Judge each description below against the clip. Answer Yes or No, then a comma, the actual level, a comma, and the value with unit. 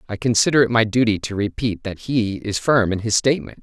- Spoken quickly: Yes, fast, 230 wpm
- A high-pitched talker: No, low, 110 Hz